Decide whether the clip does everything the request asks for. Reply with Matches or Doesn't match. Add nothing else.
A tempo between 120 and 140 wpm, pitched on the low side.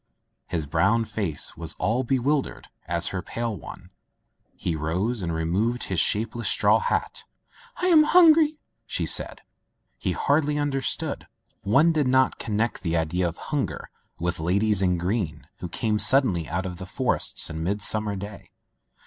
Doesn't match